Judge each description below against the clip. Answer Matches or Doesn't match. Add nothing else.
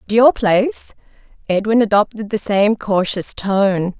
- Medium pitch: Doesn't match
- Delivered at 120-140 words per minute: Matches